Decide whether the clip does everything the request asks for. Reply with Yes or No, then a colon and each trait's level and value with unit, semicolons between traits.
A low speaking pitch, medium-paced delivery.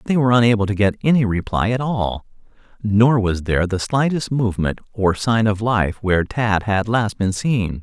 Yes: low, 110 Hz; average, 190 wpm